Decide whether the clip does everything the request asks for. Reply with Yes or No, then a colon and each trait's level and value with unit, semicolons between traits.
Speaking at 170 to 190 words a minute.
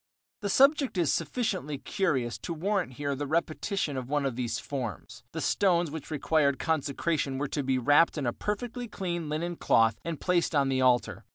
Yes: average, 185 wpm